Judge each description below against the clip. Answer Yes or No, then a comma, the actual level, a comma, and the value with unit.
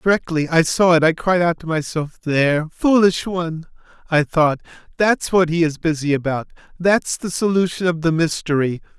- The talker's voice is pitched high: No, medium, 165 Hz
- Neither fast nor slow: Yes, average, 175 wpm